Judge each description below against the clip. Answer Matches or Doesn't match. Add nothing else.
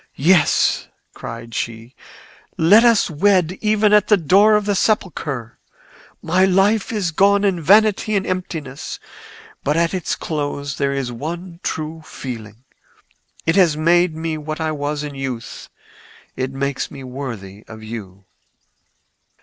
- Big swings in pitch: Matches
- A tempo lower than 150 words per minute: Matches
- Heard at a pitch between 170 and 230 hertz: Doesn't match